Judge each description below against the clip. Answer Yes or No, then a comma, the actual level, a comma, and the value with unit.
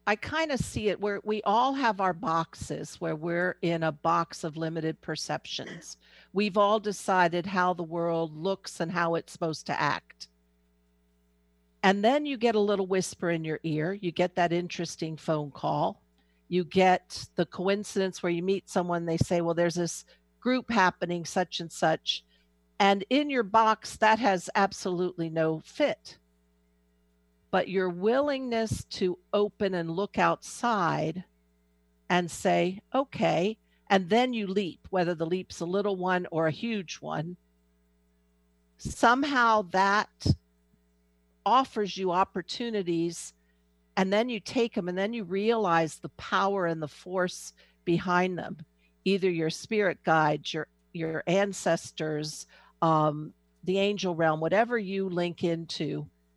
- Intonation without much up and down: No, average, 4.3 semitones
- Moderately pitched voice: Yes, medium, 175 Hz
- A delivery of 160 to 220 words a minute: No, average, 145 wpm